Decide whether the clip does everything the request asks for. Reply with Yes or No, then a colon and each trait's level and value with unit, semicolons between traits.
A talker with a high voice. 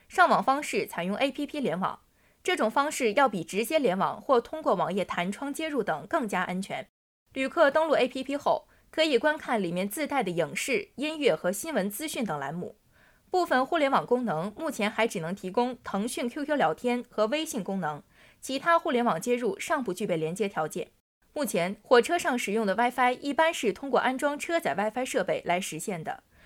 Yes: very high, 250 Hz